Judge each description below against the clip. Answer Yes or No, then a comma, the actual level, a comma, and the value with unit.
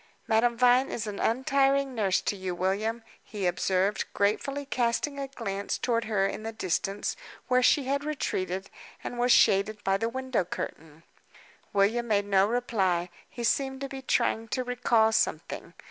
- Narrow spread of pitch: No, average, 4.3 semitones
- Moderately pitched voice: No, high, 225 Hz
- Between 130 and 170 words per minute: Yes, average, 160 wpm